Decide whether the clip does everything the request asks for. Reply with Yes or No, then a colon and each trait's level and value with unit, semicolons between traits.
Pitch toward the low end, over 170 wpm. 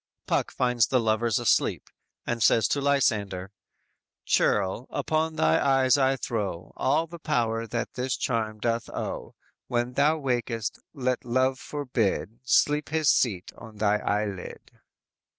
No: low, 120 Hz; average, 140 wpm